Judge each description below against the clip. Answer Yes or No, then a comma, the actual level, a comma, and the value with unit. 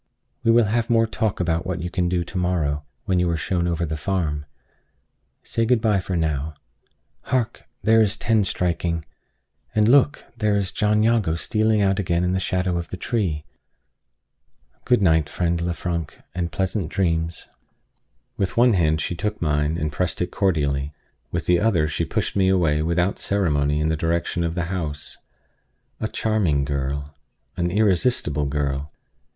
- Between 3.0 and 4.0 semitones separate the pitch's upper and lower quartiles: No, average, 4.4 semitones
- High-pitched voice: No, very low, 85 Hz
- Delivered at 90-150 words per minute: No, average, 165 wpm